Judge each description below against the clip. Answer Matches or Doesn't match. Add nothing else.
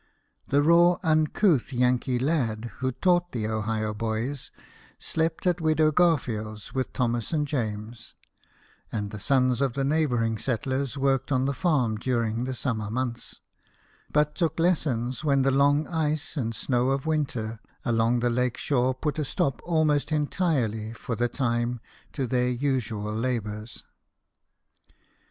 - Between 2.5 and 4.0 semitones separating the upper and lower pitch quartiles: Doesn't match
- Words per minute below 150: Matches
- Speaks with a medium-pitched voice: Doesn't match